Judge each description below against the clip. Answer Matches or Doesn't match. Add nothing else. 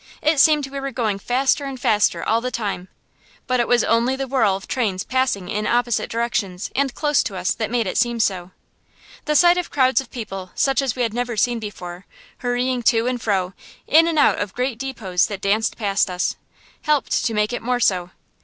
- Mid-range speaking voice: Doesn't match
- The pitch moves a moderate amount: Matches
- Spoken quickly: Matches